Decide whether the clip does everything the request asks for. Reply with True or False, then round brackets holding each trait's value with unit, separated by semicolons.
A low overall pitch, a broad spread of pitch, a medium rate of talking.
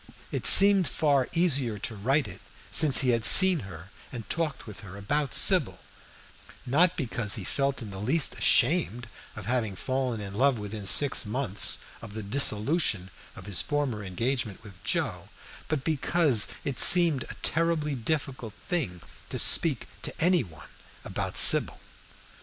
True (125 Hz; 6.3 semitones; 155 wpm)